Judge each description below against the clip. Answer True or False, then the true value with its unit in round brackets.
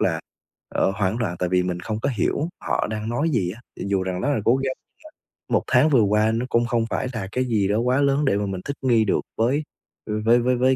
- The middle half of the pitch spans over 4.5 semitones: False (4.2 semitones)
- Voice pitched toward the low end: True (115 Hz)